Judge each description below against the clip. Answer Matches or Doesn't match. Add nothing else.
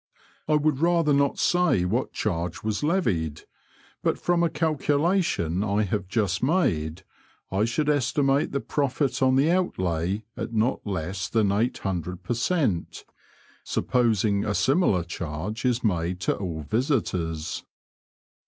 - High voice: Doesn't match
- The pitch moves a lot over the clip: Matches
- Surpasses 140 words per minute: Doesn't match